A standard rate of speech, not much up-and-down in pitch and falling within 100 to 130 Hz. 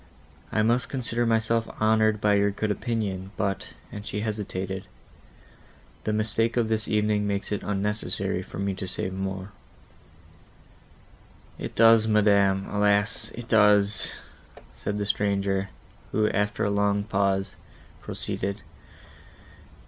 No: slow, 115 wpm; narrow, 1.6 semitones; low, 105 Hz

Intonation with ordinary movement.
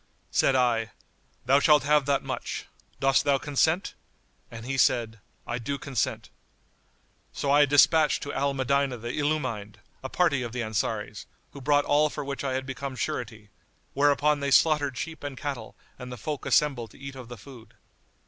Yes: average, 3.0 semitones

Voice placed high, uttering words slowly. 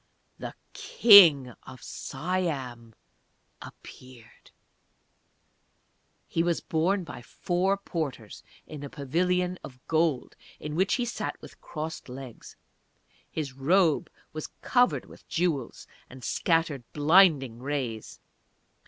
No: medium, 155 Hz; slow, 105 wpm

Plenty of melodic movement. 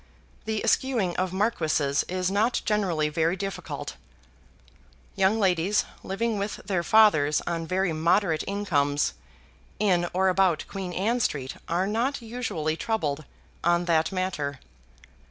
No: average, 4.2 semitones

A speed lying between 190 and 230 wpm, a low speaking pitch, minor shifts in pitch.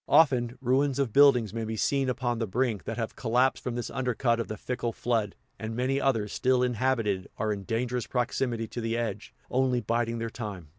Yes: average, 200 wpm; low, 120 Hz; narrow, 2.2 semitones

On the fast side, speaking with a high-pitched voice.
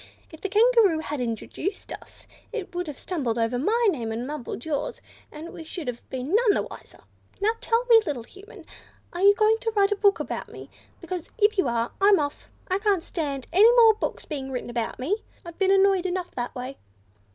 Yes: fast, 210 wpm; very high, 355 Hz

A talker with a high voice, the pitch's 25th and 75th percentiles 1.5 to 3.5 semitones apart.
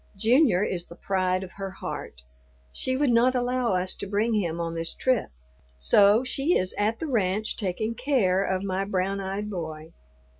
No: high, 200 Hz; average, 4.2 semitones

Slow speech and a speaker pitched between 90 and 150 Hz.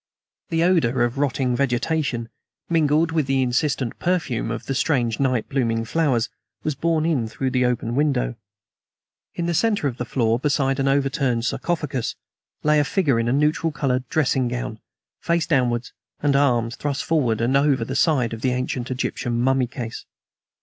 No: average, 170 wpm; low, 135 Hz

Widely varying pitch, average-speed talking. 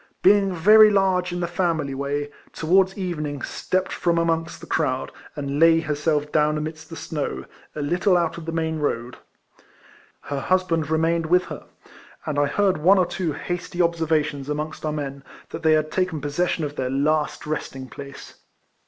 No: average, 3.2 semitones; average, 170 wpm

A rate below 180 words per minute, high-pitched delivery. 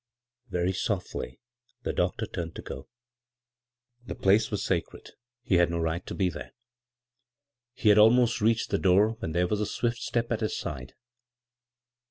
No: average, 170 wpm; low, 100 Hz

